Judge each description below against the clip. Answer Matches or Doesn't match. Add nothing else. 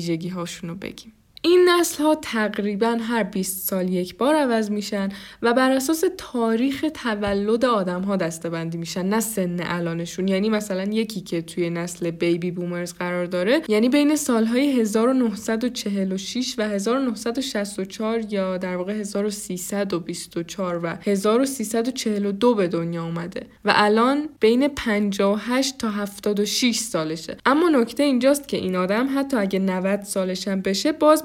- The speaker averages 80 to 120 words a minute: Doesn't match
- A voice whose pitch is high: Matches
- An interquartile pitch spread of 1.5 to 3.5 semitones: Doesn't match